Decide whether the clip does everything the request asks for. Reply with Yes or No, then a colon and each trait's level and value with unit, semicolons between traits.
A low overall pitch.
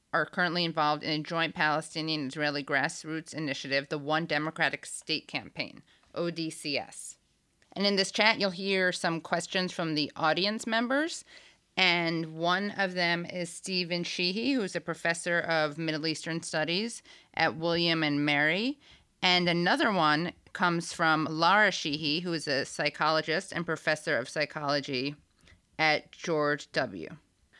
No: medium, 165 Hz